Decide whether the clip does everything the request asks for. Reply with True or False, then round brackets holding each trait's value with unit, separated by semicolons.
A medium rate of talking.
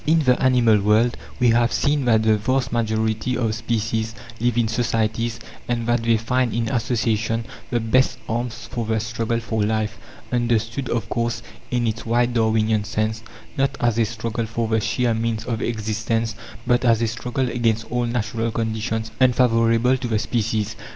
True (170 wpm)